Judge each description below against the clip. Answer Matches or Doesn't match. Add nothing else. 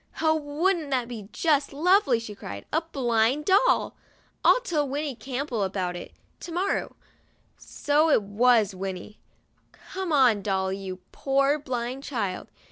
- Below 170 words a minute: Matches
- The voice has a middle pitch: Doesn't match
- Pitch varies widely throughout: Matches